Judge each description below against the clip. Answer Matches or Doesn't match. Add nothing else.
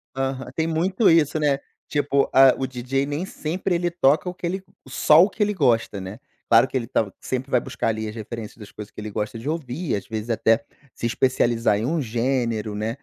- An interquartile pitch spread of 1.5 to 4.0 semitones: Doesn't match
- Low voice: Matches